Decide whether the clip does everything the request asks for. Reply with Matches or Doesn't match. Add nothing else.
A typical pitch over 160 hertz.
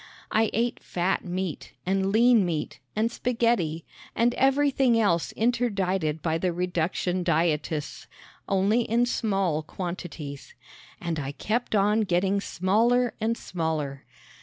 Matches